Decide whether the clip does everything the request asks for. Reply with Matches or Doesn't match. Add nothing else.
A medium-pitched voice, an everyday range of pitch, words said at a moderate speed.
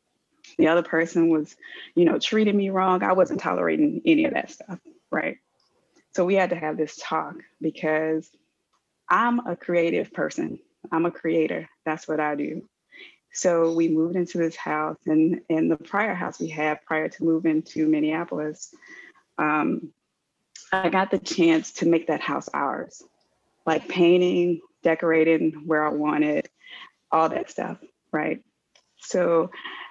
Matches